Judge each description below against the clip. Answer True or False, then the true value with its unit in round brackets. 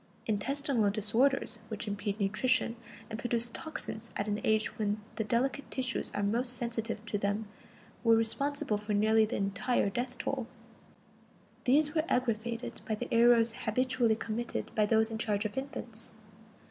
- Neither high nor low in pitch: False (225 Hz)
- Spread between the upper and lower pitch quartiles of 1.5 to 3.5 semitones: True (2.6 semitones)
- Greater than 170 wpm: False (150 wpm)